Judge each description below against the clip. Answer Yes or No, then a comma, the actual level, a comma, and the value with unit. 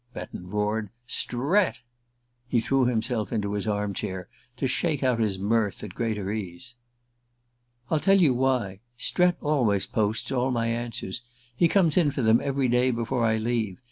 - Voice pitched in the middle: No, low, 115 Hz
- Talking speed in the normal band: Yes, average, 170 wpm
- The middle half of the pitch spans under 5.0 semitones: Yes, average, 4.0 semitones